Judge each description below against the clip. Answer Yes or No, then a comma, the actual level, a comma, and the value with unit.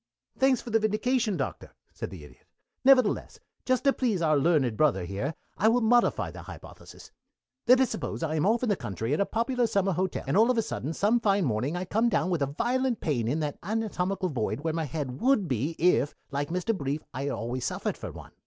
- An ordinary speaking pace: No, fast, 225 wpm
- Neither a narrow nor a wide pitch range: No, wide, 8.0 semitones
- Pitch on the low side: No, medium, 180 Hz